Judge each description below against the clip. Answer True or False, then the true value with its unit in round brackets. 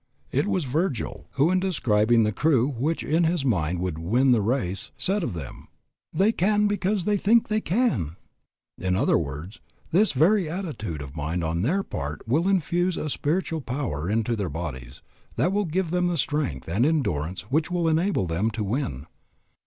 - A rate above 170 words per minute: True (180 wpm)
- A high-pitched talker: False (135 Hz)